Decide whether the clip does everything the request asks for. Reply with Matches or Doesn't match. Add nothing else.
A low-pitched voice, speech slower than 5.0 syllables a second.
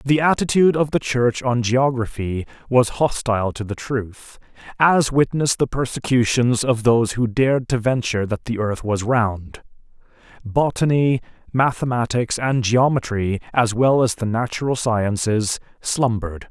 Matches